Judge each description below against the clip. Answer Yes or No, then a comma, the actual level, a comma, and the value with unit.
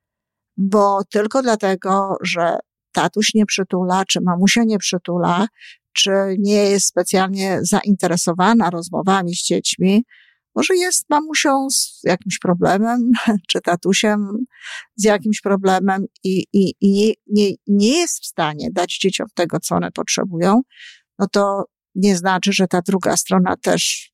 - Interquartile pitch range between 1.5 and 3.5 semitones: Yes, narrow, 2.5 semitones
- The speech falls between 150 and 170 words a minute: No, average, 135 wpm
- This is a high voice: Yes, high, 195 Hz